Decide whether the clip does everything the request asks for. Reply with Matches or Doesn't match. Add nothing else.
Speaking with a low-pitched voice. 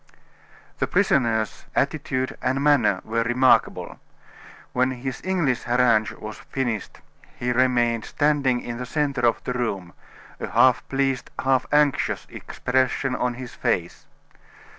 Matches